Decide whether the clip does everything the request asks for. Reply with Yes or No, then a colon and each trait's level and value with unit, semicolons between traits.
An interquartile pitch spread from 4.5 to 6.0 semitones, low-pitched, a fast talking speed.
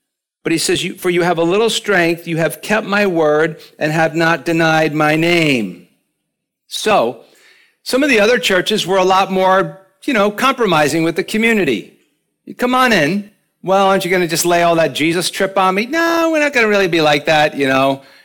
No: average, 4.9 semitones; high, 190 Hz; fast, 210 wpm